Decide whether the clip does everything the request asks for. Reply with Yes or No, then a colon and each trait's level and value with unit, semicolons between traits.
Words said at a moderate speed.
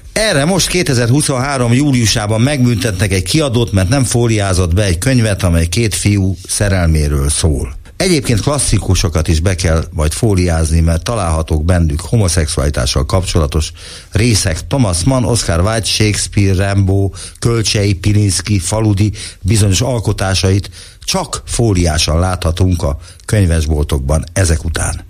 Yes: average, 115 wpm